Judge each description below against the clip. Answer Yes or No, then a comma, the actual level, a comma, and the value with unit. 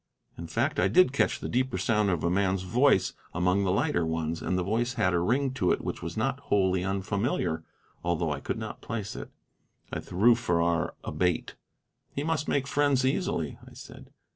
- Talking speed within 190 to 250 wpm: Yes, average, 195 wpm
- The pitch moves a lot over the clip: Yes, wide, 6.6 semitones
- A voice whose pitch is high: No, low, 100 Hz